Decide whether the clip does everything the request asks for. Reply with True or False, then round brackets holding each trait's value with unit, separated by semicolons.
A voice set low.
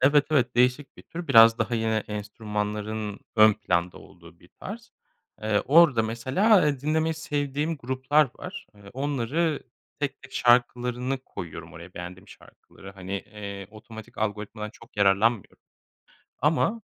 True (115 Hz)